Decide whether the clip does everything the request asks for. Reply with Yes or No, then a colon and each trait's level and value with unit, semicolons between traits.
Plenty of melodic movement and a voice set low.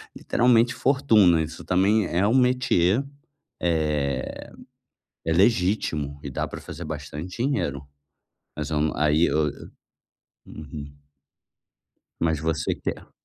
Yes: wide, 6.0 semitones; very low, 80 Hz